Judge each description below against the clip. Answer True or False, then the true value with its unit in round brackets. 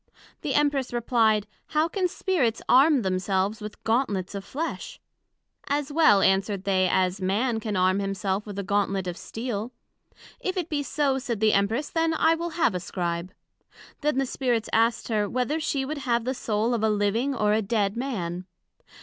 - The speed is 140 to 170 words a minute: False (180 wpm)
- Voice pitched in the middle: False (225 Hz)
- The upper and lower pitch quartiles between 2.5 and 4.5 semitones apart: False (5.6 semitones)